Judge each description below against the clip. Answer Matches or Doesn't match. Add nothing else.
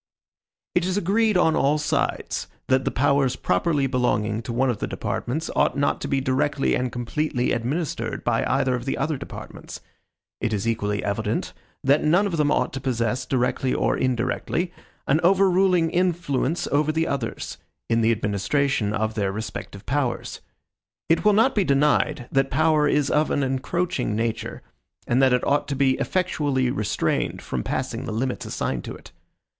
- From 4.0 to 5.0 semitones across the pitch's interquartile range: Matches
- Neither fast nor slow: Matches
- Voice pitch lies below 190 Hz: Matches